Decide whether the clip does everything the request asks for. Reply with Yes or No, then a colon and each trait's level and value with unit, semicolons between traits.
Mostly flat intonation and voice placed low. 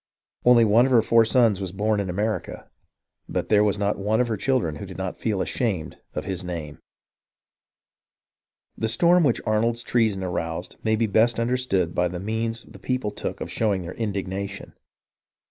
No: average, 3.4 semitones; low, 105 Hz